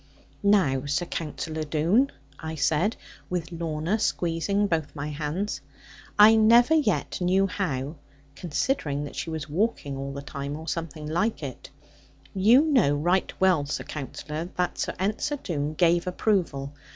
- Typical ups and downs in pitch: Yes, average, 5.0 semitones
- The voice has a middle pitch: Yes, medium, 165 Hz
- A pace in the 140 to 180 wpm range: Yes, average, 145 wpm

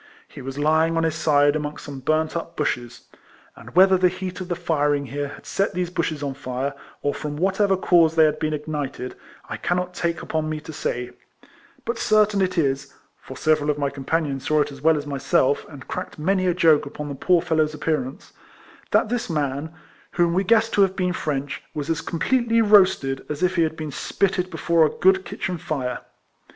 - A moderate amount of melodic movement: Yes, average, 3.9 semitones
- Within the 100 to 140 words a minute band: No, fast, 205 wpm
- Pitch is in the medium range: Yes, medium, 155 Hz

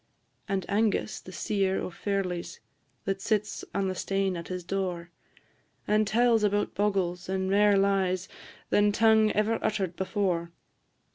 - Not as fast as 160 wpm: Yes, average, 140 wpm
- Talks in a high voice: Yes, high, 195 Hz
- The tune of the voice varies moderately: No, narrow, 2.1 semitones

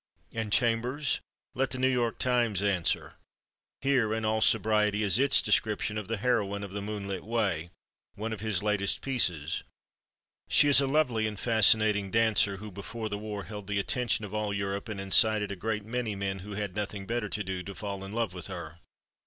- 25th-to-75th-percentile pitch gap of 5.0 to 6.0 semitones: No, narrow, 2.4 semitones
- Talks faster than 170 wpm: Yes, average, 195 wpm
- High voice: No, low, 105 Hz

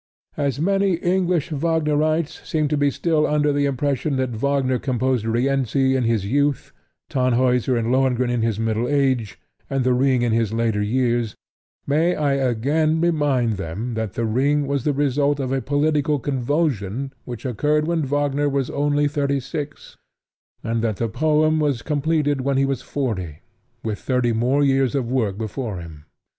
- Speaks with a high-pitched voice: No, low, 135 Hz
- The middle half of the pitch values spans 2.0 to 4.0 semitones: Yes, average, 3.5 semitones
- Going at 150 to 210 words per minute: Yes, average, 165 wpm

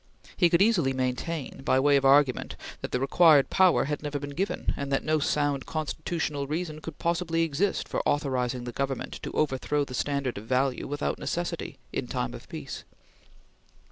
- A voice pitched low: No, medium, 145 Hz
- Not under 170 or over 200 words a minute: Yes, average, 175 wpm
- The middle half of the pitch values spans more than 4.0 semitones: No, average, 3.2 semitones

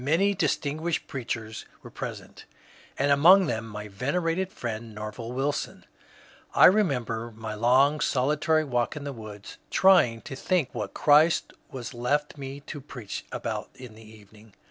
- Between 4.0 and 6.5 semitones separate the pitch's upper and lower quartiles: Yes, average, 5.1 semitones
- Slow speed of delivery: No, average, 150 wpm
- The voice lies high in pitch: No, low, 130 Hz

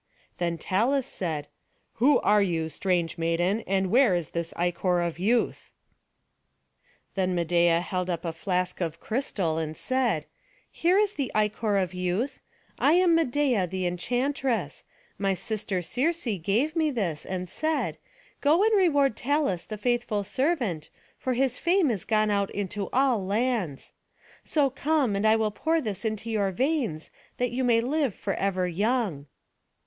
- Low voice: No, high, 210 Hz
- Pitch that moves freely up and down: Yes, wide, 6.5 semitones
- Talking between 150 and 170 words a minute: Yes, average, 155 wpm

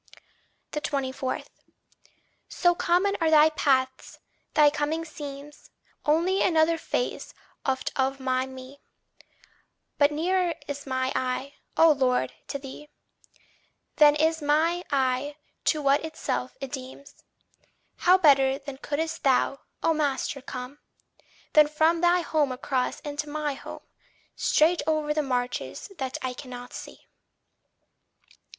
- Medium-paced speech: No, slow, 120 wpm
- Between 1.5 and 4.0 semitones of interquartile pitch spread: Yes, average, 3.0 semitones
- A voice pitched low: No, very high, 290 Hz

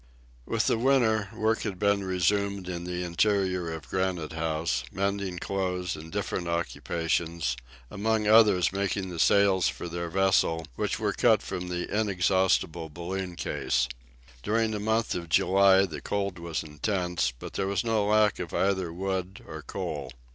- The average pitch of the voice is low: Yes, very low, 95 Hz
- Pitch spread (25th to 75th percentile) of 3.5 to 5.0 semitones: No, average, 2.8 semitones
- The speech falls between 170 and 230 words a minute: No, average, 155 wpm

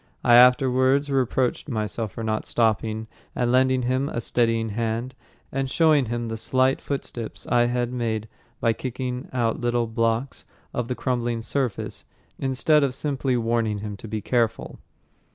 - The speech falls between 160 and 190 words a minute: No, average, 150 wpm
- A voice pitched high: No, low, 120 Hz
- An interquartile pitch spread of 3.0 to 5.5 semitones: No, narrow, 2.4 semitones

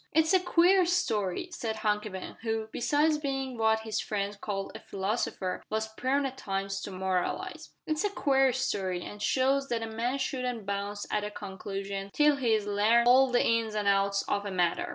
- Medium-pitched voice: No, high, 220 Hz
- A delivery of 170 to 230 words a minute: Yes, average, 190 wpm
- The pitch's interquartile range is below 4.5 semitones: No, average, 5.0 semitones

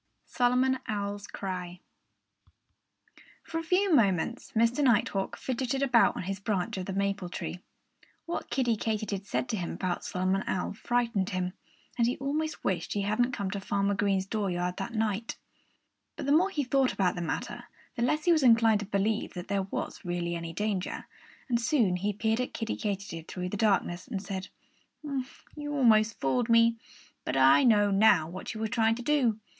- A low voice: No, high, 210 Hz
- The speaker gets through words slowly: No, average, 180 wpm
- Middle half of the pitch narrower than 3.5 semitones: No, average, 4.2 semitones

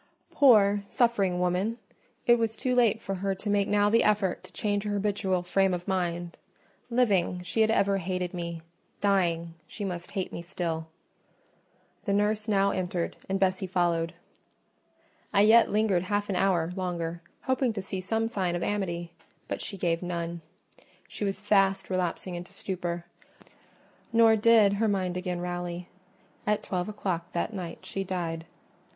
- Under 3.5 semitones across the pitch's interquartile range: Yes, average, 2.8 semitones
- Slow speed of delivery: No, average, 155 wpm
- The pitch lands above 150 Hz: Yes, high, 190 Hz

